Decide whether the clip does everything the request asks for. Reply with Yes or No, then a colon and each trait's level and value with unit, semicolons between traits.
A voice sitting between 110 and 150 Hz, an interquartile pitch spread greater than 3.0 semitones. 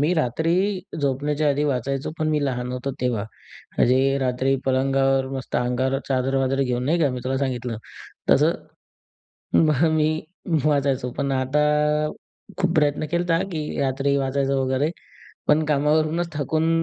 No: medium, 140 Hz; narrow, 2.5 semitones